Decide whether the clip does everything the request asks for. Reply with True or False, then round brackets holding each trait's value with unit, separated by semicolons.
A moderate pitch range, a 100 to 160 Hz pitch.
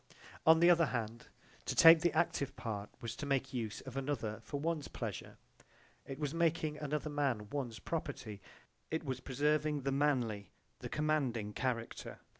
True (4.4 semitones; 140 Hz)